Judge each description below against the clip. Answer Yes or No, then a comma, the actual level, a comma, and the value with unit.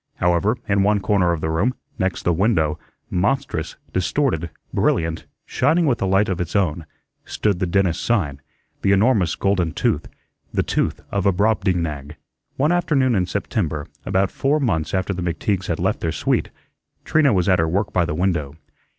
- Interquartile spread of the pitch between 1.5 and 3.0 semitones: No, average, 3.9 semitones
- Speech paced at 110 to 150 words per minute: No, average, 175 wpm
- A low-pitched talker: Yes, very low, 95 Hz